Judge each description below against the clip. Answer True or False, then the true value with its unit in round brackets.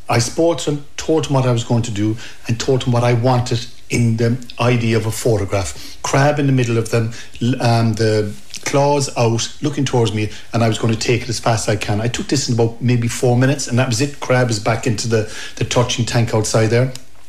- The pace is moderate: False (245 wpm)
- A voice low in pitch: True (120 Hz)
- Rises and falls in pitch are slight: True (2.0 semitones)